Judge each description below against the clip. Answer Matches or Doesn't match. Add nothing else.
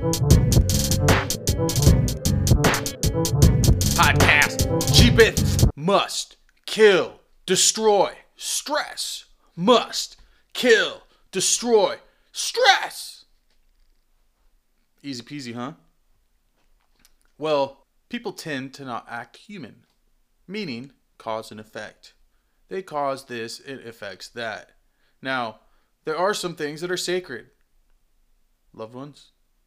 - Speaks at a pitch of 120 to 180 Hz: Matches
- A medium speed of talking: Doesn't match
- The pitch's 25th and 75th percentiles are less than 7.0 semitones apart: Doesn't match